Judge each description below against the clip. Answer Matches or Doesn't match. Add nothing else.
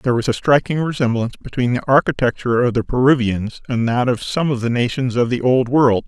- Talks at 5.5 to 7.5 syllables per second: Matches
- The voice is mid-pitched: Doesn't match